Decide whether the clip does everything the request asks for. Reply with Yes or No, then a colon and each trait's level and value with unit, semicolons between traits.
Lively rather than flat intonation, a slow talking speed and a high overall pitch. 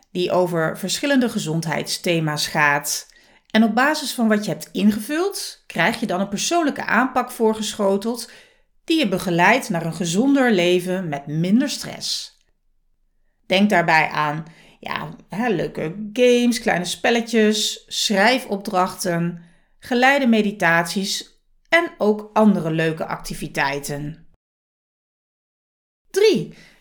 Yes: wide, 6.0 semitones; slow, 105 wpm; high, 205 Hz